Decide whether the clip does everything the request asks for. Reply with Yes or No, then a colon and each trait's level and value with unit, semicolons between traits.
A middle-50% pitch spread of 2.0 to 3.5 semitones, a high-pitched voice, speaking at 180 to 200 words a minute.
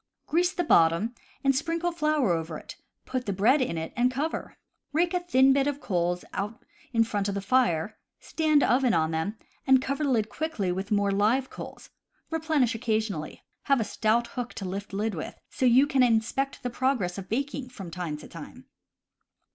No: wide, 5.6 semitones; high, 235 Hz; average, 190 wpm